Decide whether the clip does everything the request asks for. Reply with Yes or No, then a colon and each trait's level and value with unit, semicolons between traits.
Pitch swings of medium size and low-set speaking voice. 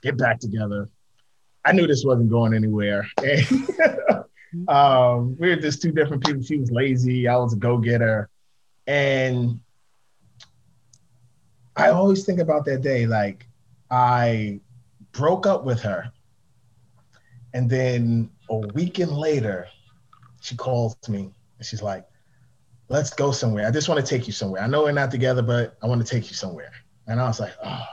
Yes: average, 3.3 semitones; low, 125 Hz